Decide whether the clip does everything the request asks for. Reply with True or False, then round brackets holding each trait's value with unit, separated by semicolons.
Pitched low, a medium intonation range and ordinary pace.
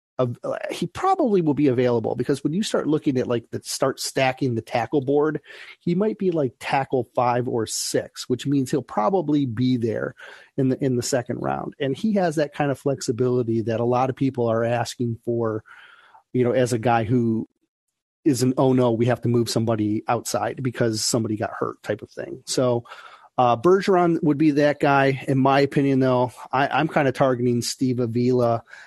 True (130 Hz; 3.3 semitones; 195 wpm)